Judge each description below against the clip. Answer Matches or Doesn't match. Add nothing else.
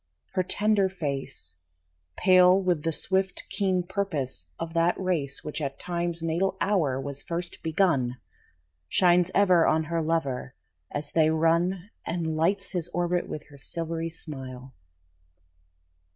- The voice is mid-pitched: Matches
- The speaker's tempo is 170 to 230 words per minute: Doesn't match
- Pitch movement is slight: Doesn't match